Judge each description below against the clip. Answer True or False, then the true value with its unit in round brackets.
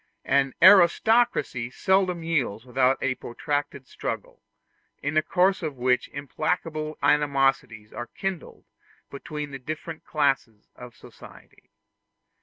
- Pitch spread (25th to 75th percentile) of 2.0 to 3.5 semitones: False (4.2 semitones)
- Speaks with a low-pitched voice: False (145 Hz)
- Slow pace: True (110 wpm)